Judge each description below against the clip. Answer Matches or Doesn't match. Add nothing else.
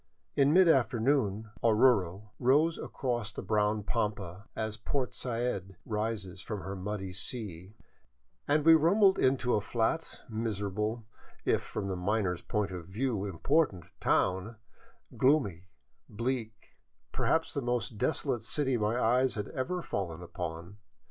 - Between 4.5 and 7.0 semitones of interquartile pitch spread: Matches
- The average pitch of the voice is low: Matches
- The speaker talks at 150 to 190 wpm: Doesn't match